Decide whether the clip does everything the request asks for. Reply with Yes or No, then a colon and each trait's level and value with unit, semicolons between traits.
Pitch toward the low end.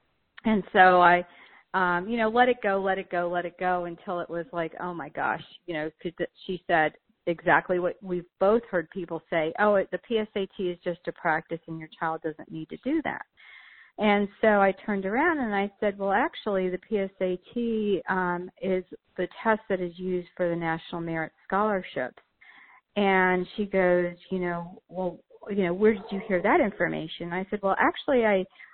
No: medium, 185 Hz